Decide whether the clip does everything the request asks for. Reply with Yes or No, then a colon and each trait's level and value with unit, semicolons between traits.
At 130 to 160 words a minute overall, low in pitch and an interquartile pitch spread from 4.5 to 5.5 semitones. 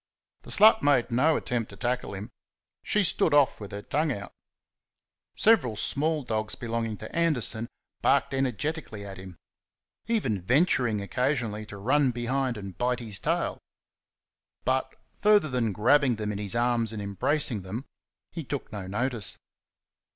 Yes: average, 150 wpm; low, 120 Hz; average, 5.1 semitones